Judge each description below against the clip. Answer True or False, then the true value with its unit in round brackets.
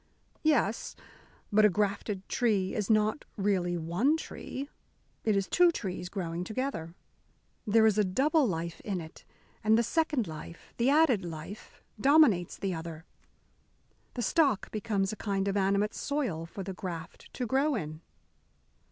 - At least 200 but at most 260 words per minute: False (150 wpm)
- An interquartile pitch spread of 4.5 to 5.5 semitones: True (5.2 semitones)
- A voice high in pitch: True (205 Hz)